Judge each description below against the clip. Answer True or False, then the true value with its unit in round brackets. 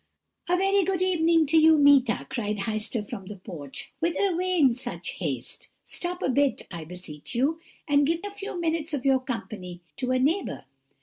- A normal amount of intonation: False (7.7 semitones)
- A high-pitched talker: True (285 Hz)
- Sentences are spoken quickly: False (185 wpm)